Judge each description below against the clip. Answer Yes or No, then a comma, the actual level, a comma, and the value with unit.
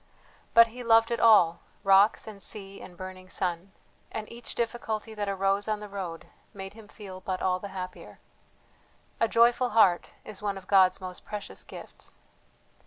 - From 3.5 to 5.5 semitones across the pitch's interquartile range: No, average, 2.9 semitones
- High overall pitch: Yes, high, 200 Hz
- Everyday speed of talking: Yes, average, 170 wpm